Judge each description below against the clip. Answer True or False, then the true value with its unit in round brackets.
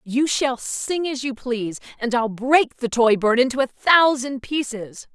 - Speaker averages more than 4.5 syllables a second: False (4.2 syllables/s)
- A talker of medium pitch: False (250 Hz)